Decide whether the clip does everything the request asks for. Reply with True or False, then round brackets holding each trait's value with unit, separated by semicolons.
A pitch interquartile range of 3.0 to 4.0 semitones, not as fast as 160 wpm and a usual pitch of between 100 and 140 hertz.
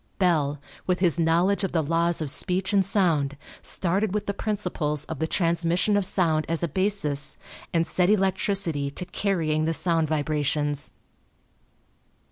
False (3.5 semitones; 150 wpm; 170 Hz)